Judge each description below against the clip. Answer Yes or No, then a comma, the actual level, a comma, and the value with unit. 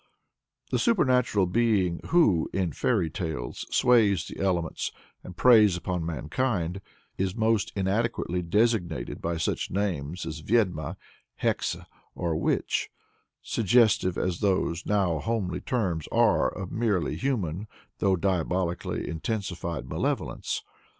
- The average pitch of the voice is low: Yes, very low, 95 Hz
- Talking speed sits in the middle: No, slow, 115 wpm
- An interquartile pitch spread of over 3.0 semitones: Yes, average, 4.7 semitones